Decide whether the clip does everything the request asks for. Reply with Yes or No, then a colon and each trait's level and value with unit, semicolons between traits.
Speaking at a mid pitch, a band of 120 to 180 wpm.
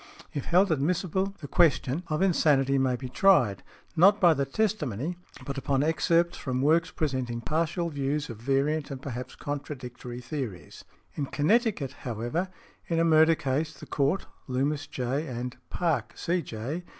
Yes: medium, 145 Hz; average, 150 wpm